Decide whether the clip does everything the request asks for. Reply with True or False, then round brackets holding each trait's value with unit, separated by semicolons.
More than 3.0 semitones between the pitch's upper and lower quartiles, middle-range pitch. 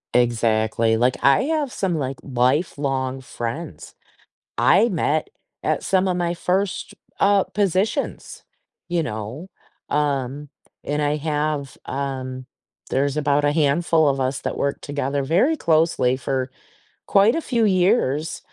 True (5.0 semitones; 145 Hz)